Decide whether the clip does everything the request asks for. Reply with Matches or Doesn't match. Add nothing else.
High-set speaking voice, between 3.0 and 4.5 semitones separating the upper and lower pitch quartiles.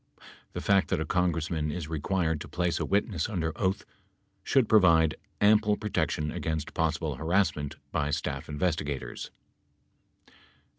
Doesn't match